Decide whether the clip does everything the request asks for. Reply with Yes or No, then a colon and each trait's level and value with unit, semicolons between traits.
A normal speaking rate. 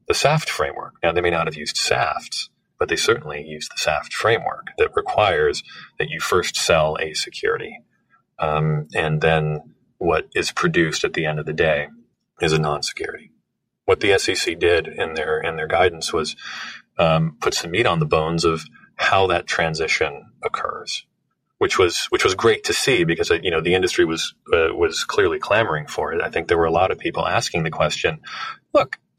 Yes: average, 190 wpm